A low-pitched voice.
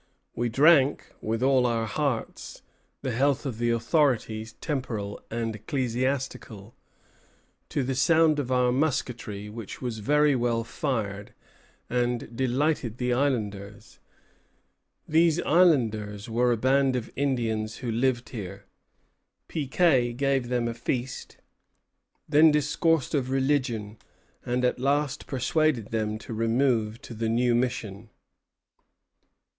Yes: low, 125 Hz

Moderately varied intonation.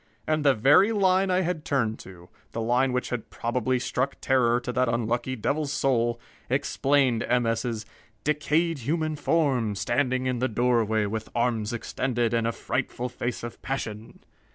Yes: average, 3.2 semitones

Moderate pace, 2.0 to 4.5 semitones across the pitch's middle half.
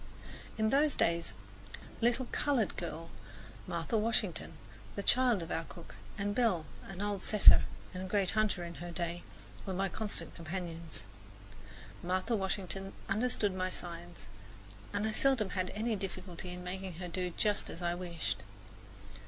Yes: average, 155 wpm; average, 3.5 semitones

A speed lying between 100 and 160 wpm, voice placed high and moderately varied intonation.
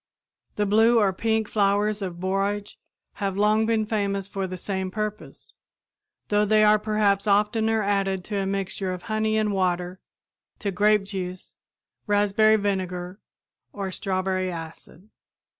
No: average, 140 wpm; high, 200 Hz; narrow, 2.0 semitones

